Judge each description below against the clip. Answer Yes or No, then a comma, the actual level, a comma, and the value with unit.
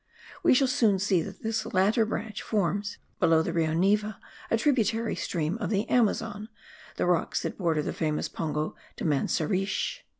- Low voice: No, high, 200 Hz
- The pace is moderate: Yes, average, 165 wpm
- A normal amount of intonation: Yes, average, 4.9 semitones